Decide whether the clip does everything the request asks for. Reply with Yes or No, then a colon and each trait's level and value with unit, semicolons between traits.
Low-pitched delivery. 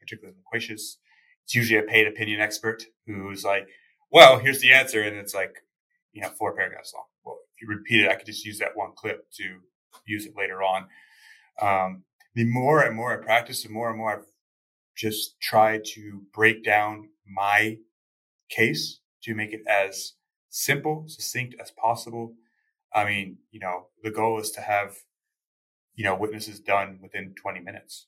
Yes: low, 110 Hz